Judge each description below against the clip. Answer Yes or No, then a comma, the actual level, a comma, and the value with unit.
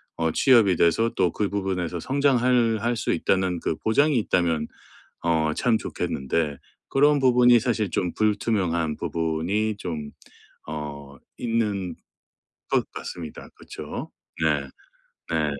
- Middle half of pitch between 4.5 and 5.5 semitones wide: No, wide, 6.1 semitones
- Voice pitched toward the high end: No, very low, 95 Hz